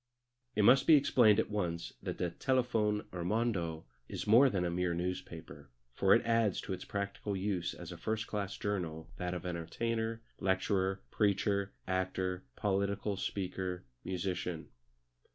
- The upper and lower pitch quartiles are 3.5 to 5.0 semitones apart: No, average, 2.9 semitones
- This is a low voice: Yes, very low, 95 Hz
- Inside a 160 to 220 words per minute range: No, average, 145 wpm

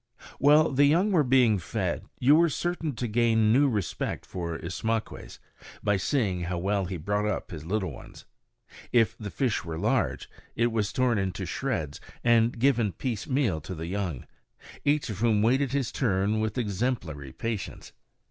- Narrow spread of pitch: No, average, 5.3 semitones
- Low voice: Yes, low, 110 Hz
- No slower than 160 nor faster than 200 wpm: Yes, average, 165 wpm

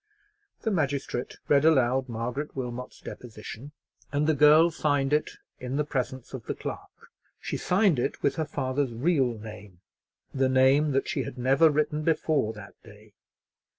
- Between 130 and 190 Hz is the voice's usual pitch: Yes, low, 135 Hz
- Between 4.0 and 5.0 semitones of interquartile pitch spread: No, average, 3.6 semitones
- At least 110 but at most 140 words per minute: No, average, 155 wpm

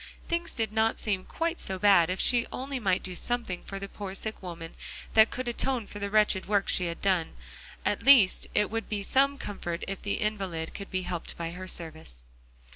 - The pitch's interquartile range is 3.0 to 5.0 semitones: Yes, average, 3.6 semitones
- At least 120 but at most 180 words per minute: No, fast, 205 wpm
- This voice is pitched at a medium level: No, high, 200 Hz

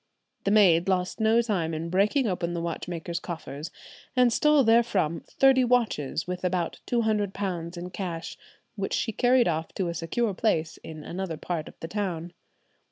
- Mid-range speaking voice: Yes, medium, 180 Hz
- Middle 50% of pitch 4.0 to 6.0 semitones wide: Yes, average, 4.7 semitones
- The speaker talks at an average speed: Yes, average, 170 wpm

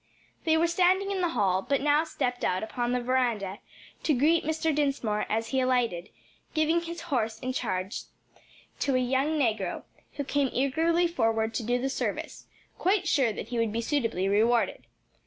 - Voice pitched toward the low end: No, very high, 255 Hz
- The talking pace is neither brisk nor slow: Yes, average, 175 wpm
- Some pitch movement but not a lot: No, wide, 5.8 semitones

